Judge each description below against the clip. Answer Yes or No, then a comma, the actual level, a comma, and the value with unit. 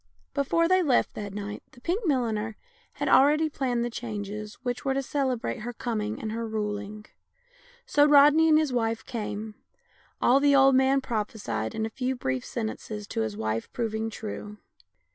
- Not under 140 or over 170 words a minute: No, average, 180 wpm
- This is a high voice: Yes, high, 230 Hz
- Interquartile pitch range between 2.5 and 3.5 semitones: No, average, 4.3 semitones